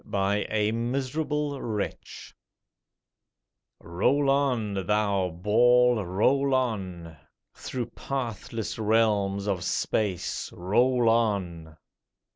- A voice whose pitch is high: No, low, 110 Hz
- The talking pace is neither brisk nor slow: No, slow, 85 wpm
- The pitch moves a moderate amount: Yes, average, 4.0 semitones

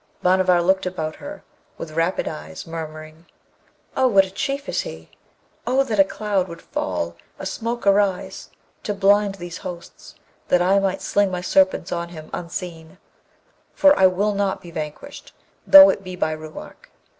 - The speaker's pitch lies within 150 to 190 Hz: Yes, medium, 185 Hz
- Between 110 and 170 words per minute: Yes, average, 165 wpm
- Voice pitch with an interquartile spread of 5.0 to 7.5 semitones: No, average, 3.3 semitones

